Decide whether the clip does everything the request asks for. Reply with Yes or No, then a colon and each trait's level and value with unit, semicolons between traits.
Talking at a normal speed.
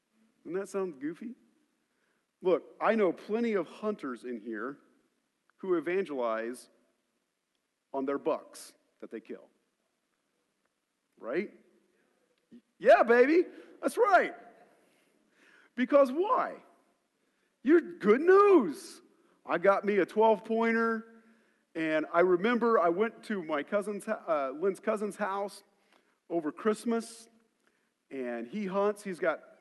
No: slow, 110 wpm